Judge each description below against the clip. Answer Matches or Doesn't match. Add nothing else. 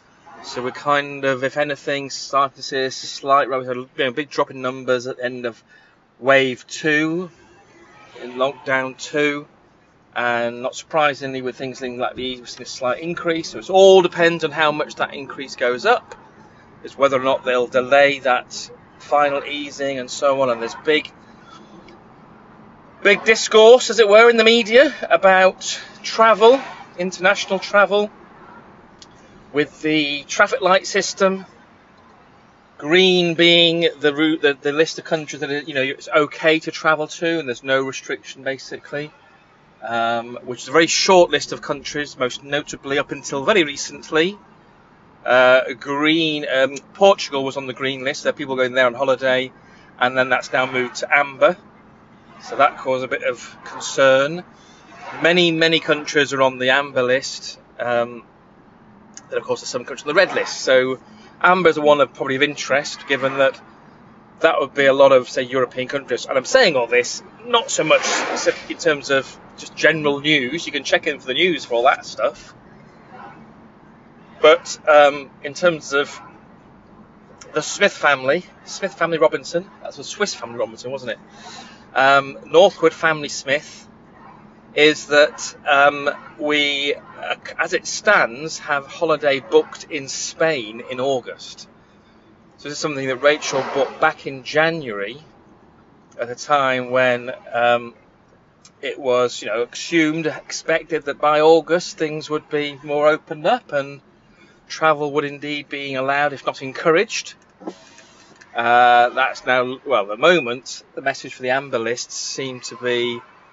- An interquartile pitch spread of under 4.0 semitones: Matches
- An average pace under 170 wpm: Matches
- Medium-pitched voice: Matches